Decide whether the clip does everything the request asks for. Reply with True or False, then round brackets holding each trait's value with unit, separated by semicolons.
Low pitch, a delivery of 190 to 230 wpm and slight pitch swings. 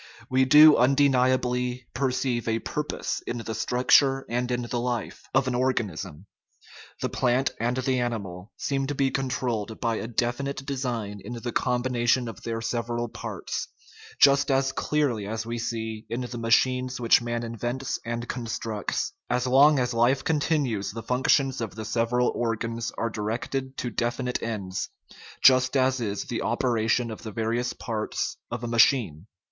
False (120 Hz; 165 wpm; 2.2 semitones)